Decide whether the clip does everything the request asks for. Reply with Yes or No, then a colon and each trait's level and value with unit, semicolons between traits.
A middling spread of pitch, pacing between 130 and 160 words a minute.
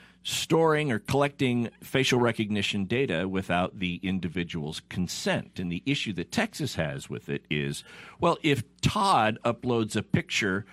No: wide, 7.2 semitones; average, 140 wpm